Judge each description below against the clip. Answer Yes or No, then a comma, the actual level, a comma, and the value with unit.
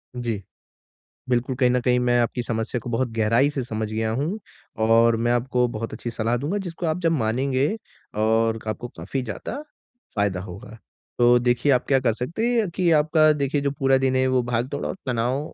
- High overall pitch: No, low, 125 Hz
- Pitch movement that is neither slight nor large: Yes, average, 3.2 semitones